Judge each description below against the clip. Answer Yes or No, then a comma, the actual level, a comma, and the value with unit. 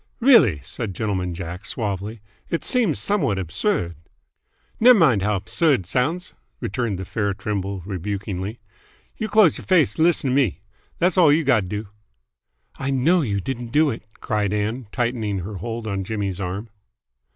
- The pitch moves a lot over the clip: Yes, wide, 6.7 semitones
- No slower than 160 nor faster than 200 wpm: Yes, average, 165 wpm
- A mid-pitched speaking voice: No, low, 110 Hz